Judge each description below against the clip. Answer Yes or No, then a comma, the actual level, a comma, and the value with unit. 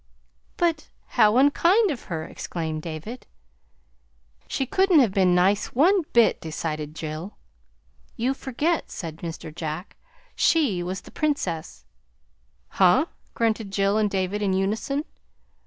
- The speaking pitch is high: Yes, high, 205 Hz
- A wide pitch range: Yes, wide, 8.1 semitones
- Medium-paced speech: No, slow, 125 wpm